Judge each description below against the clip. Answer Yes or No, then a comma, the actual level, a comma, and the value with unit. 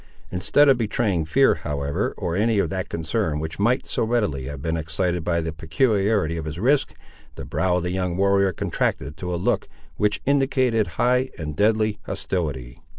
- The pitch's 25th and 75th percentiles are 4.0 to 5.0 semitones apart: No, wide, 5.4 semitones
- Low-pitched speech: Yes, very low, 95 Hz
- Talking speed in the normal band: Yes, average, 180 wpm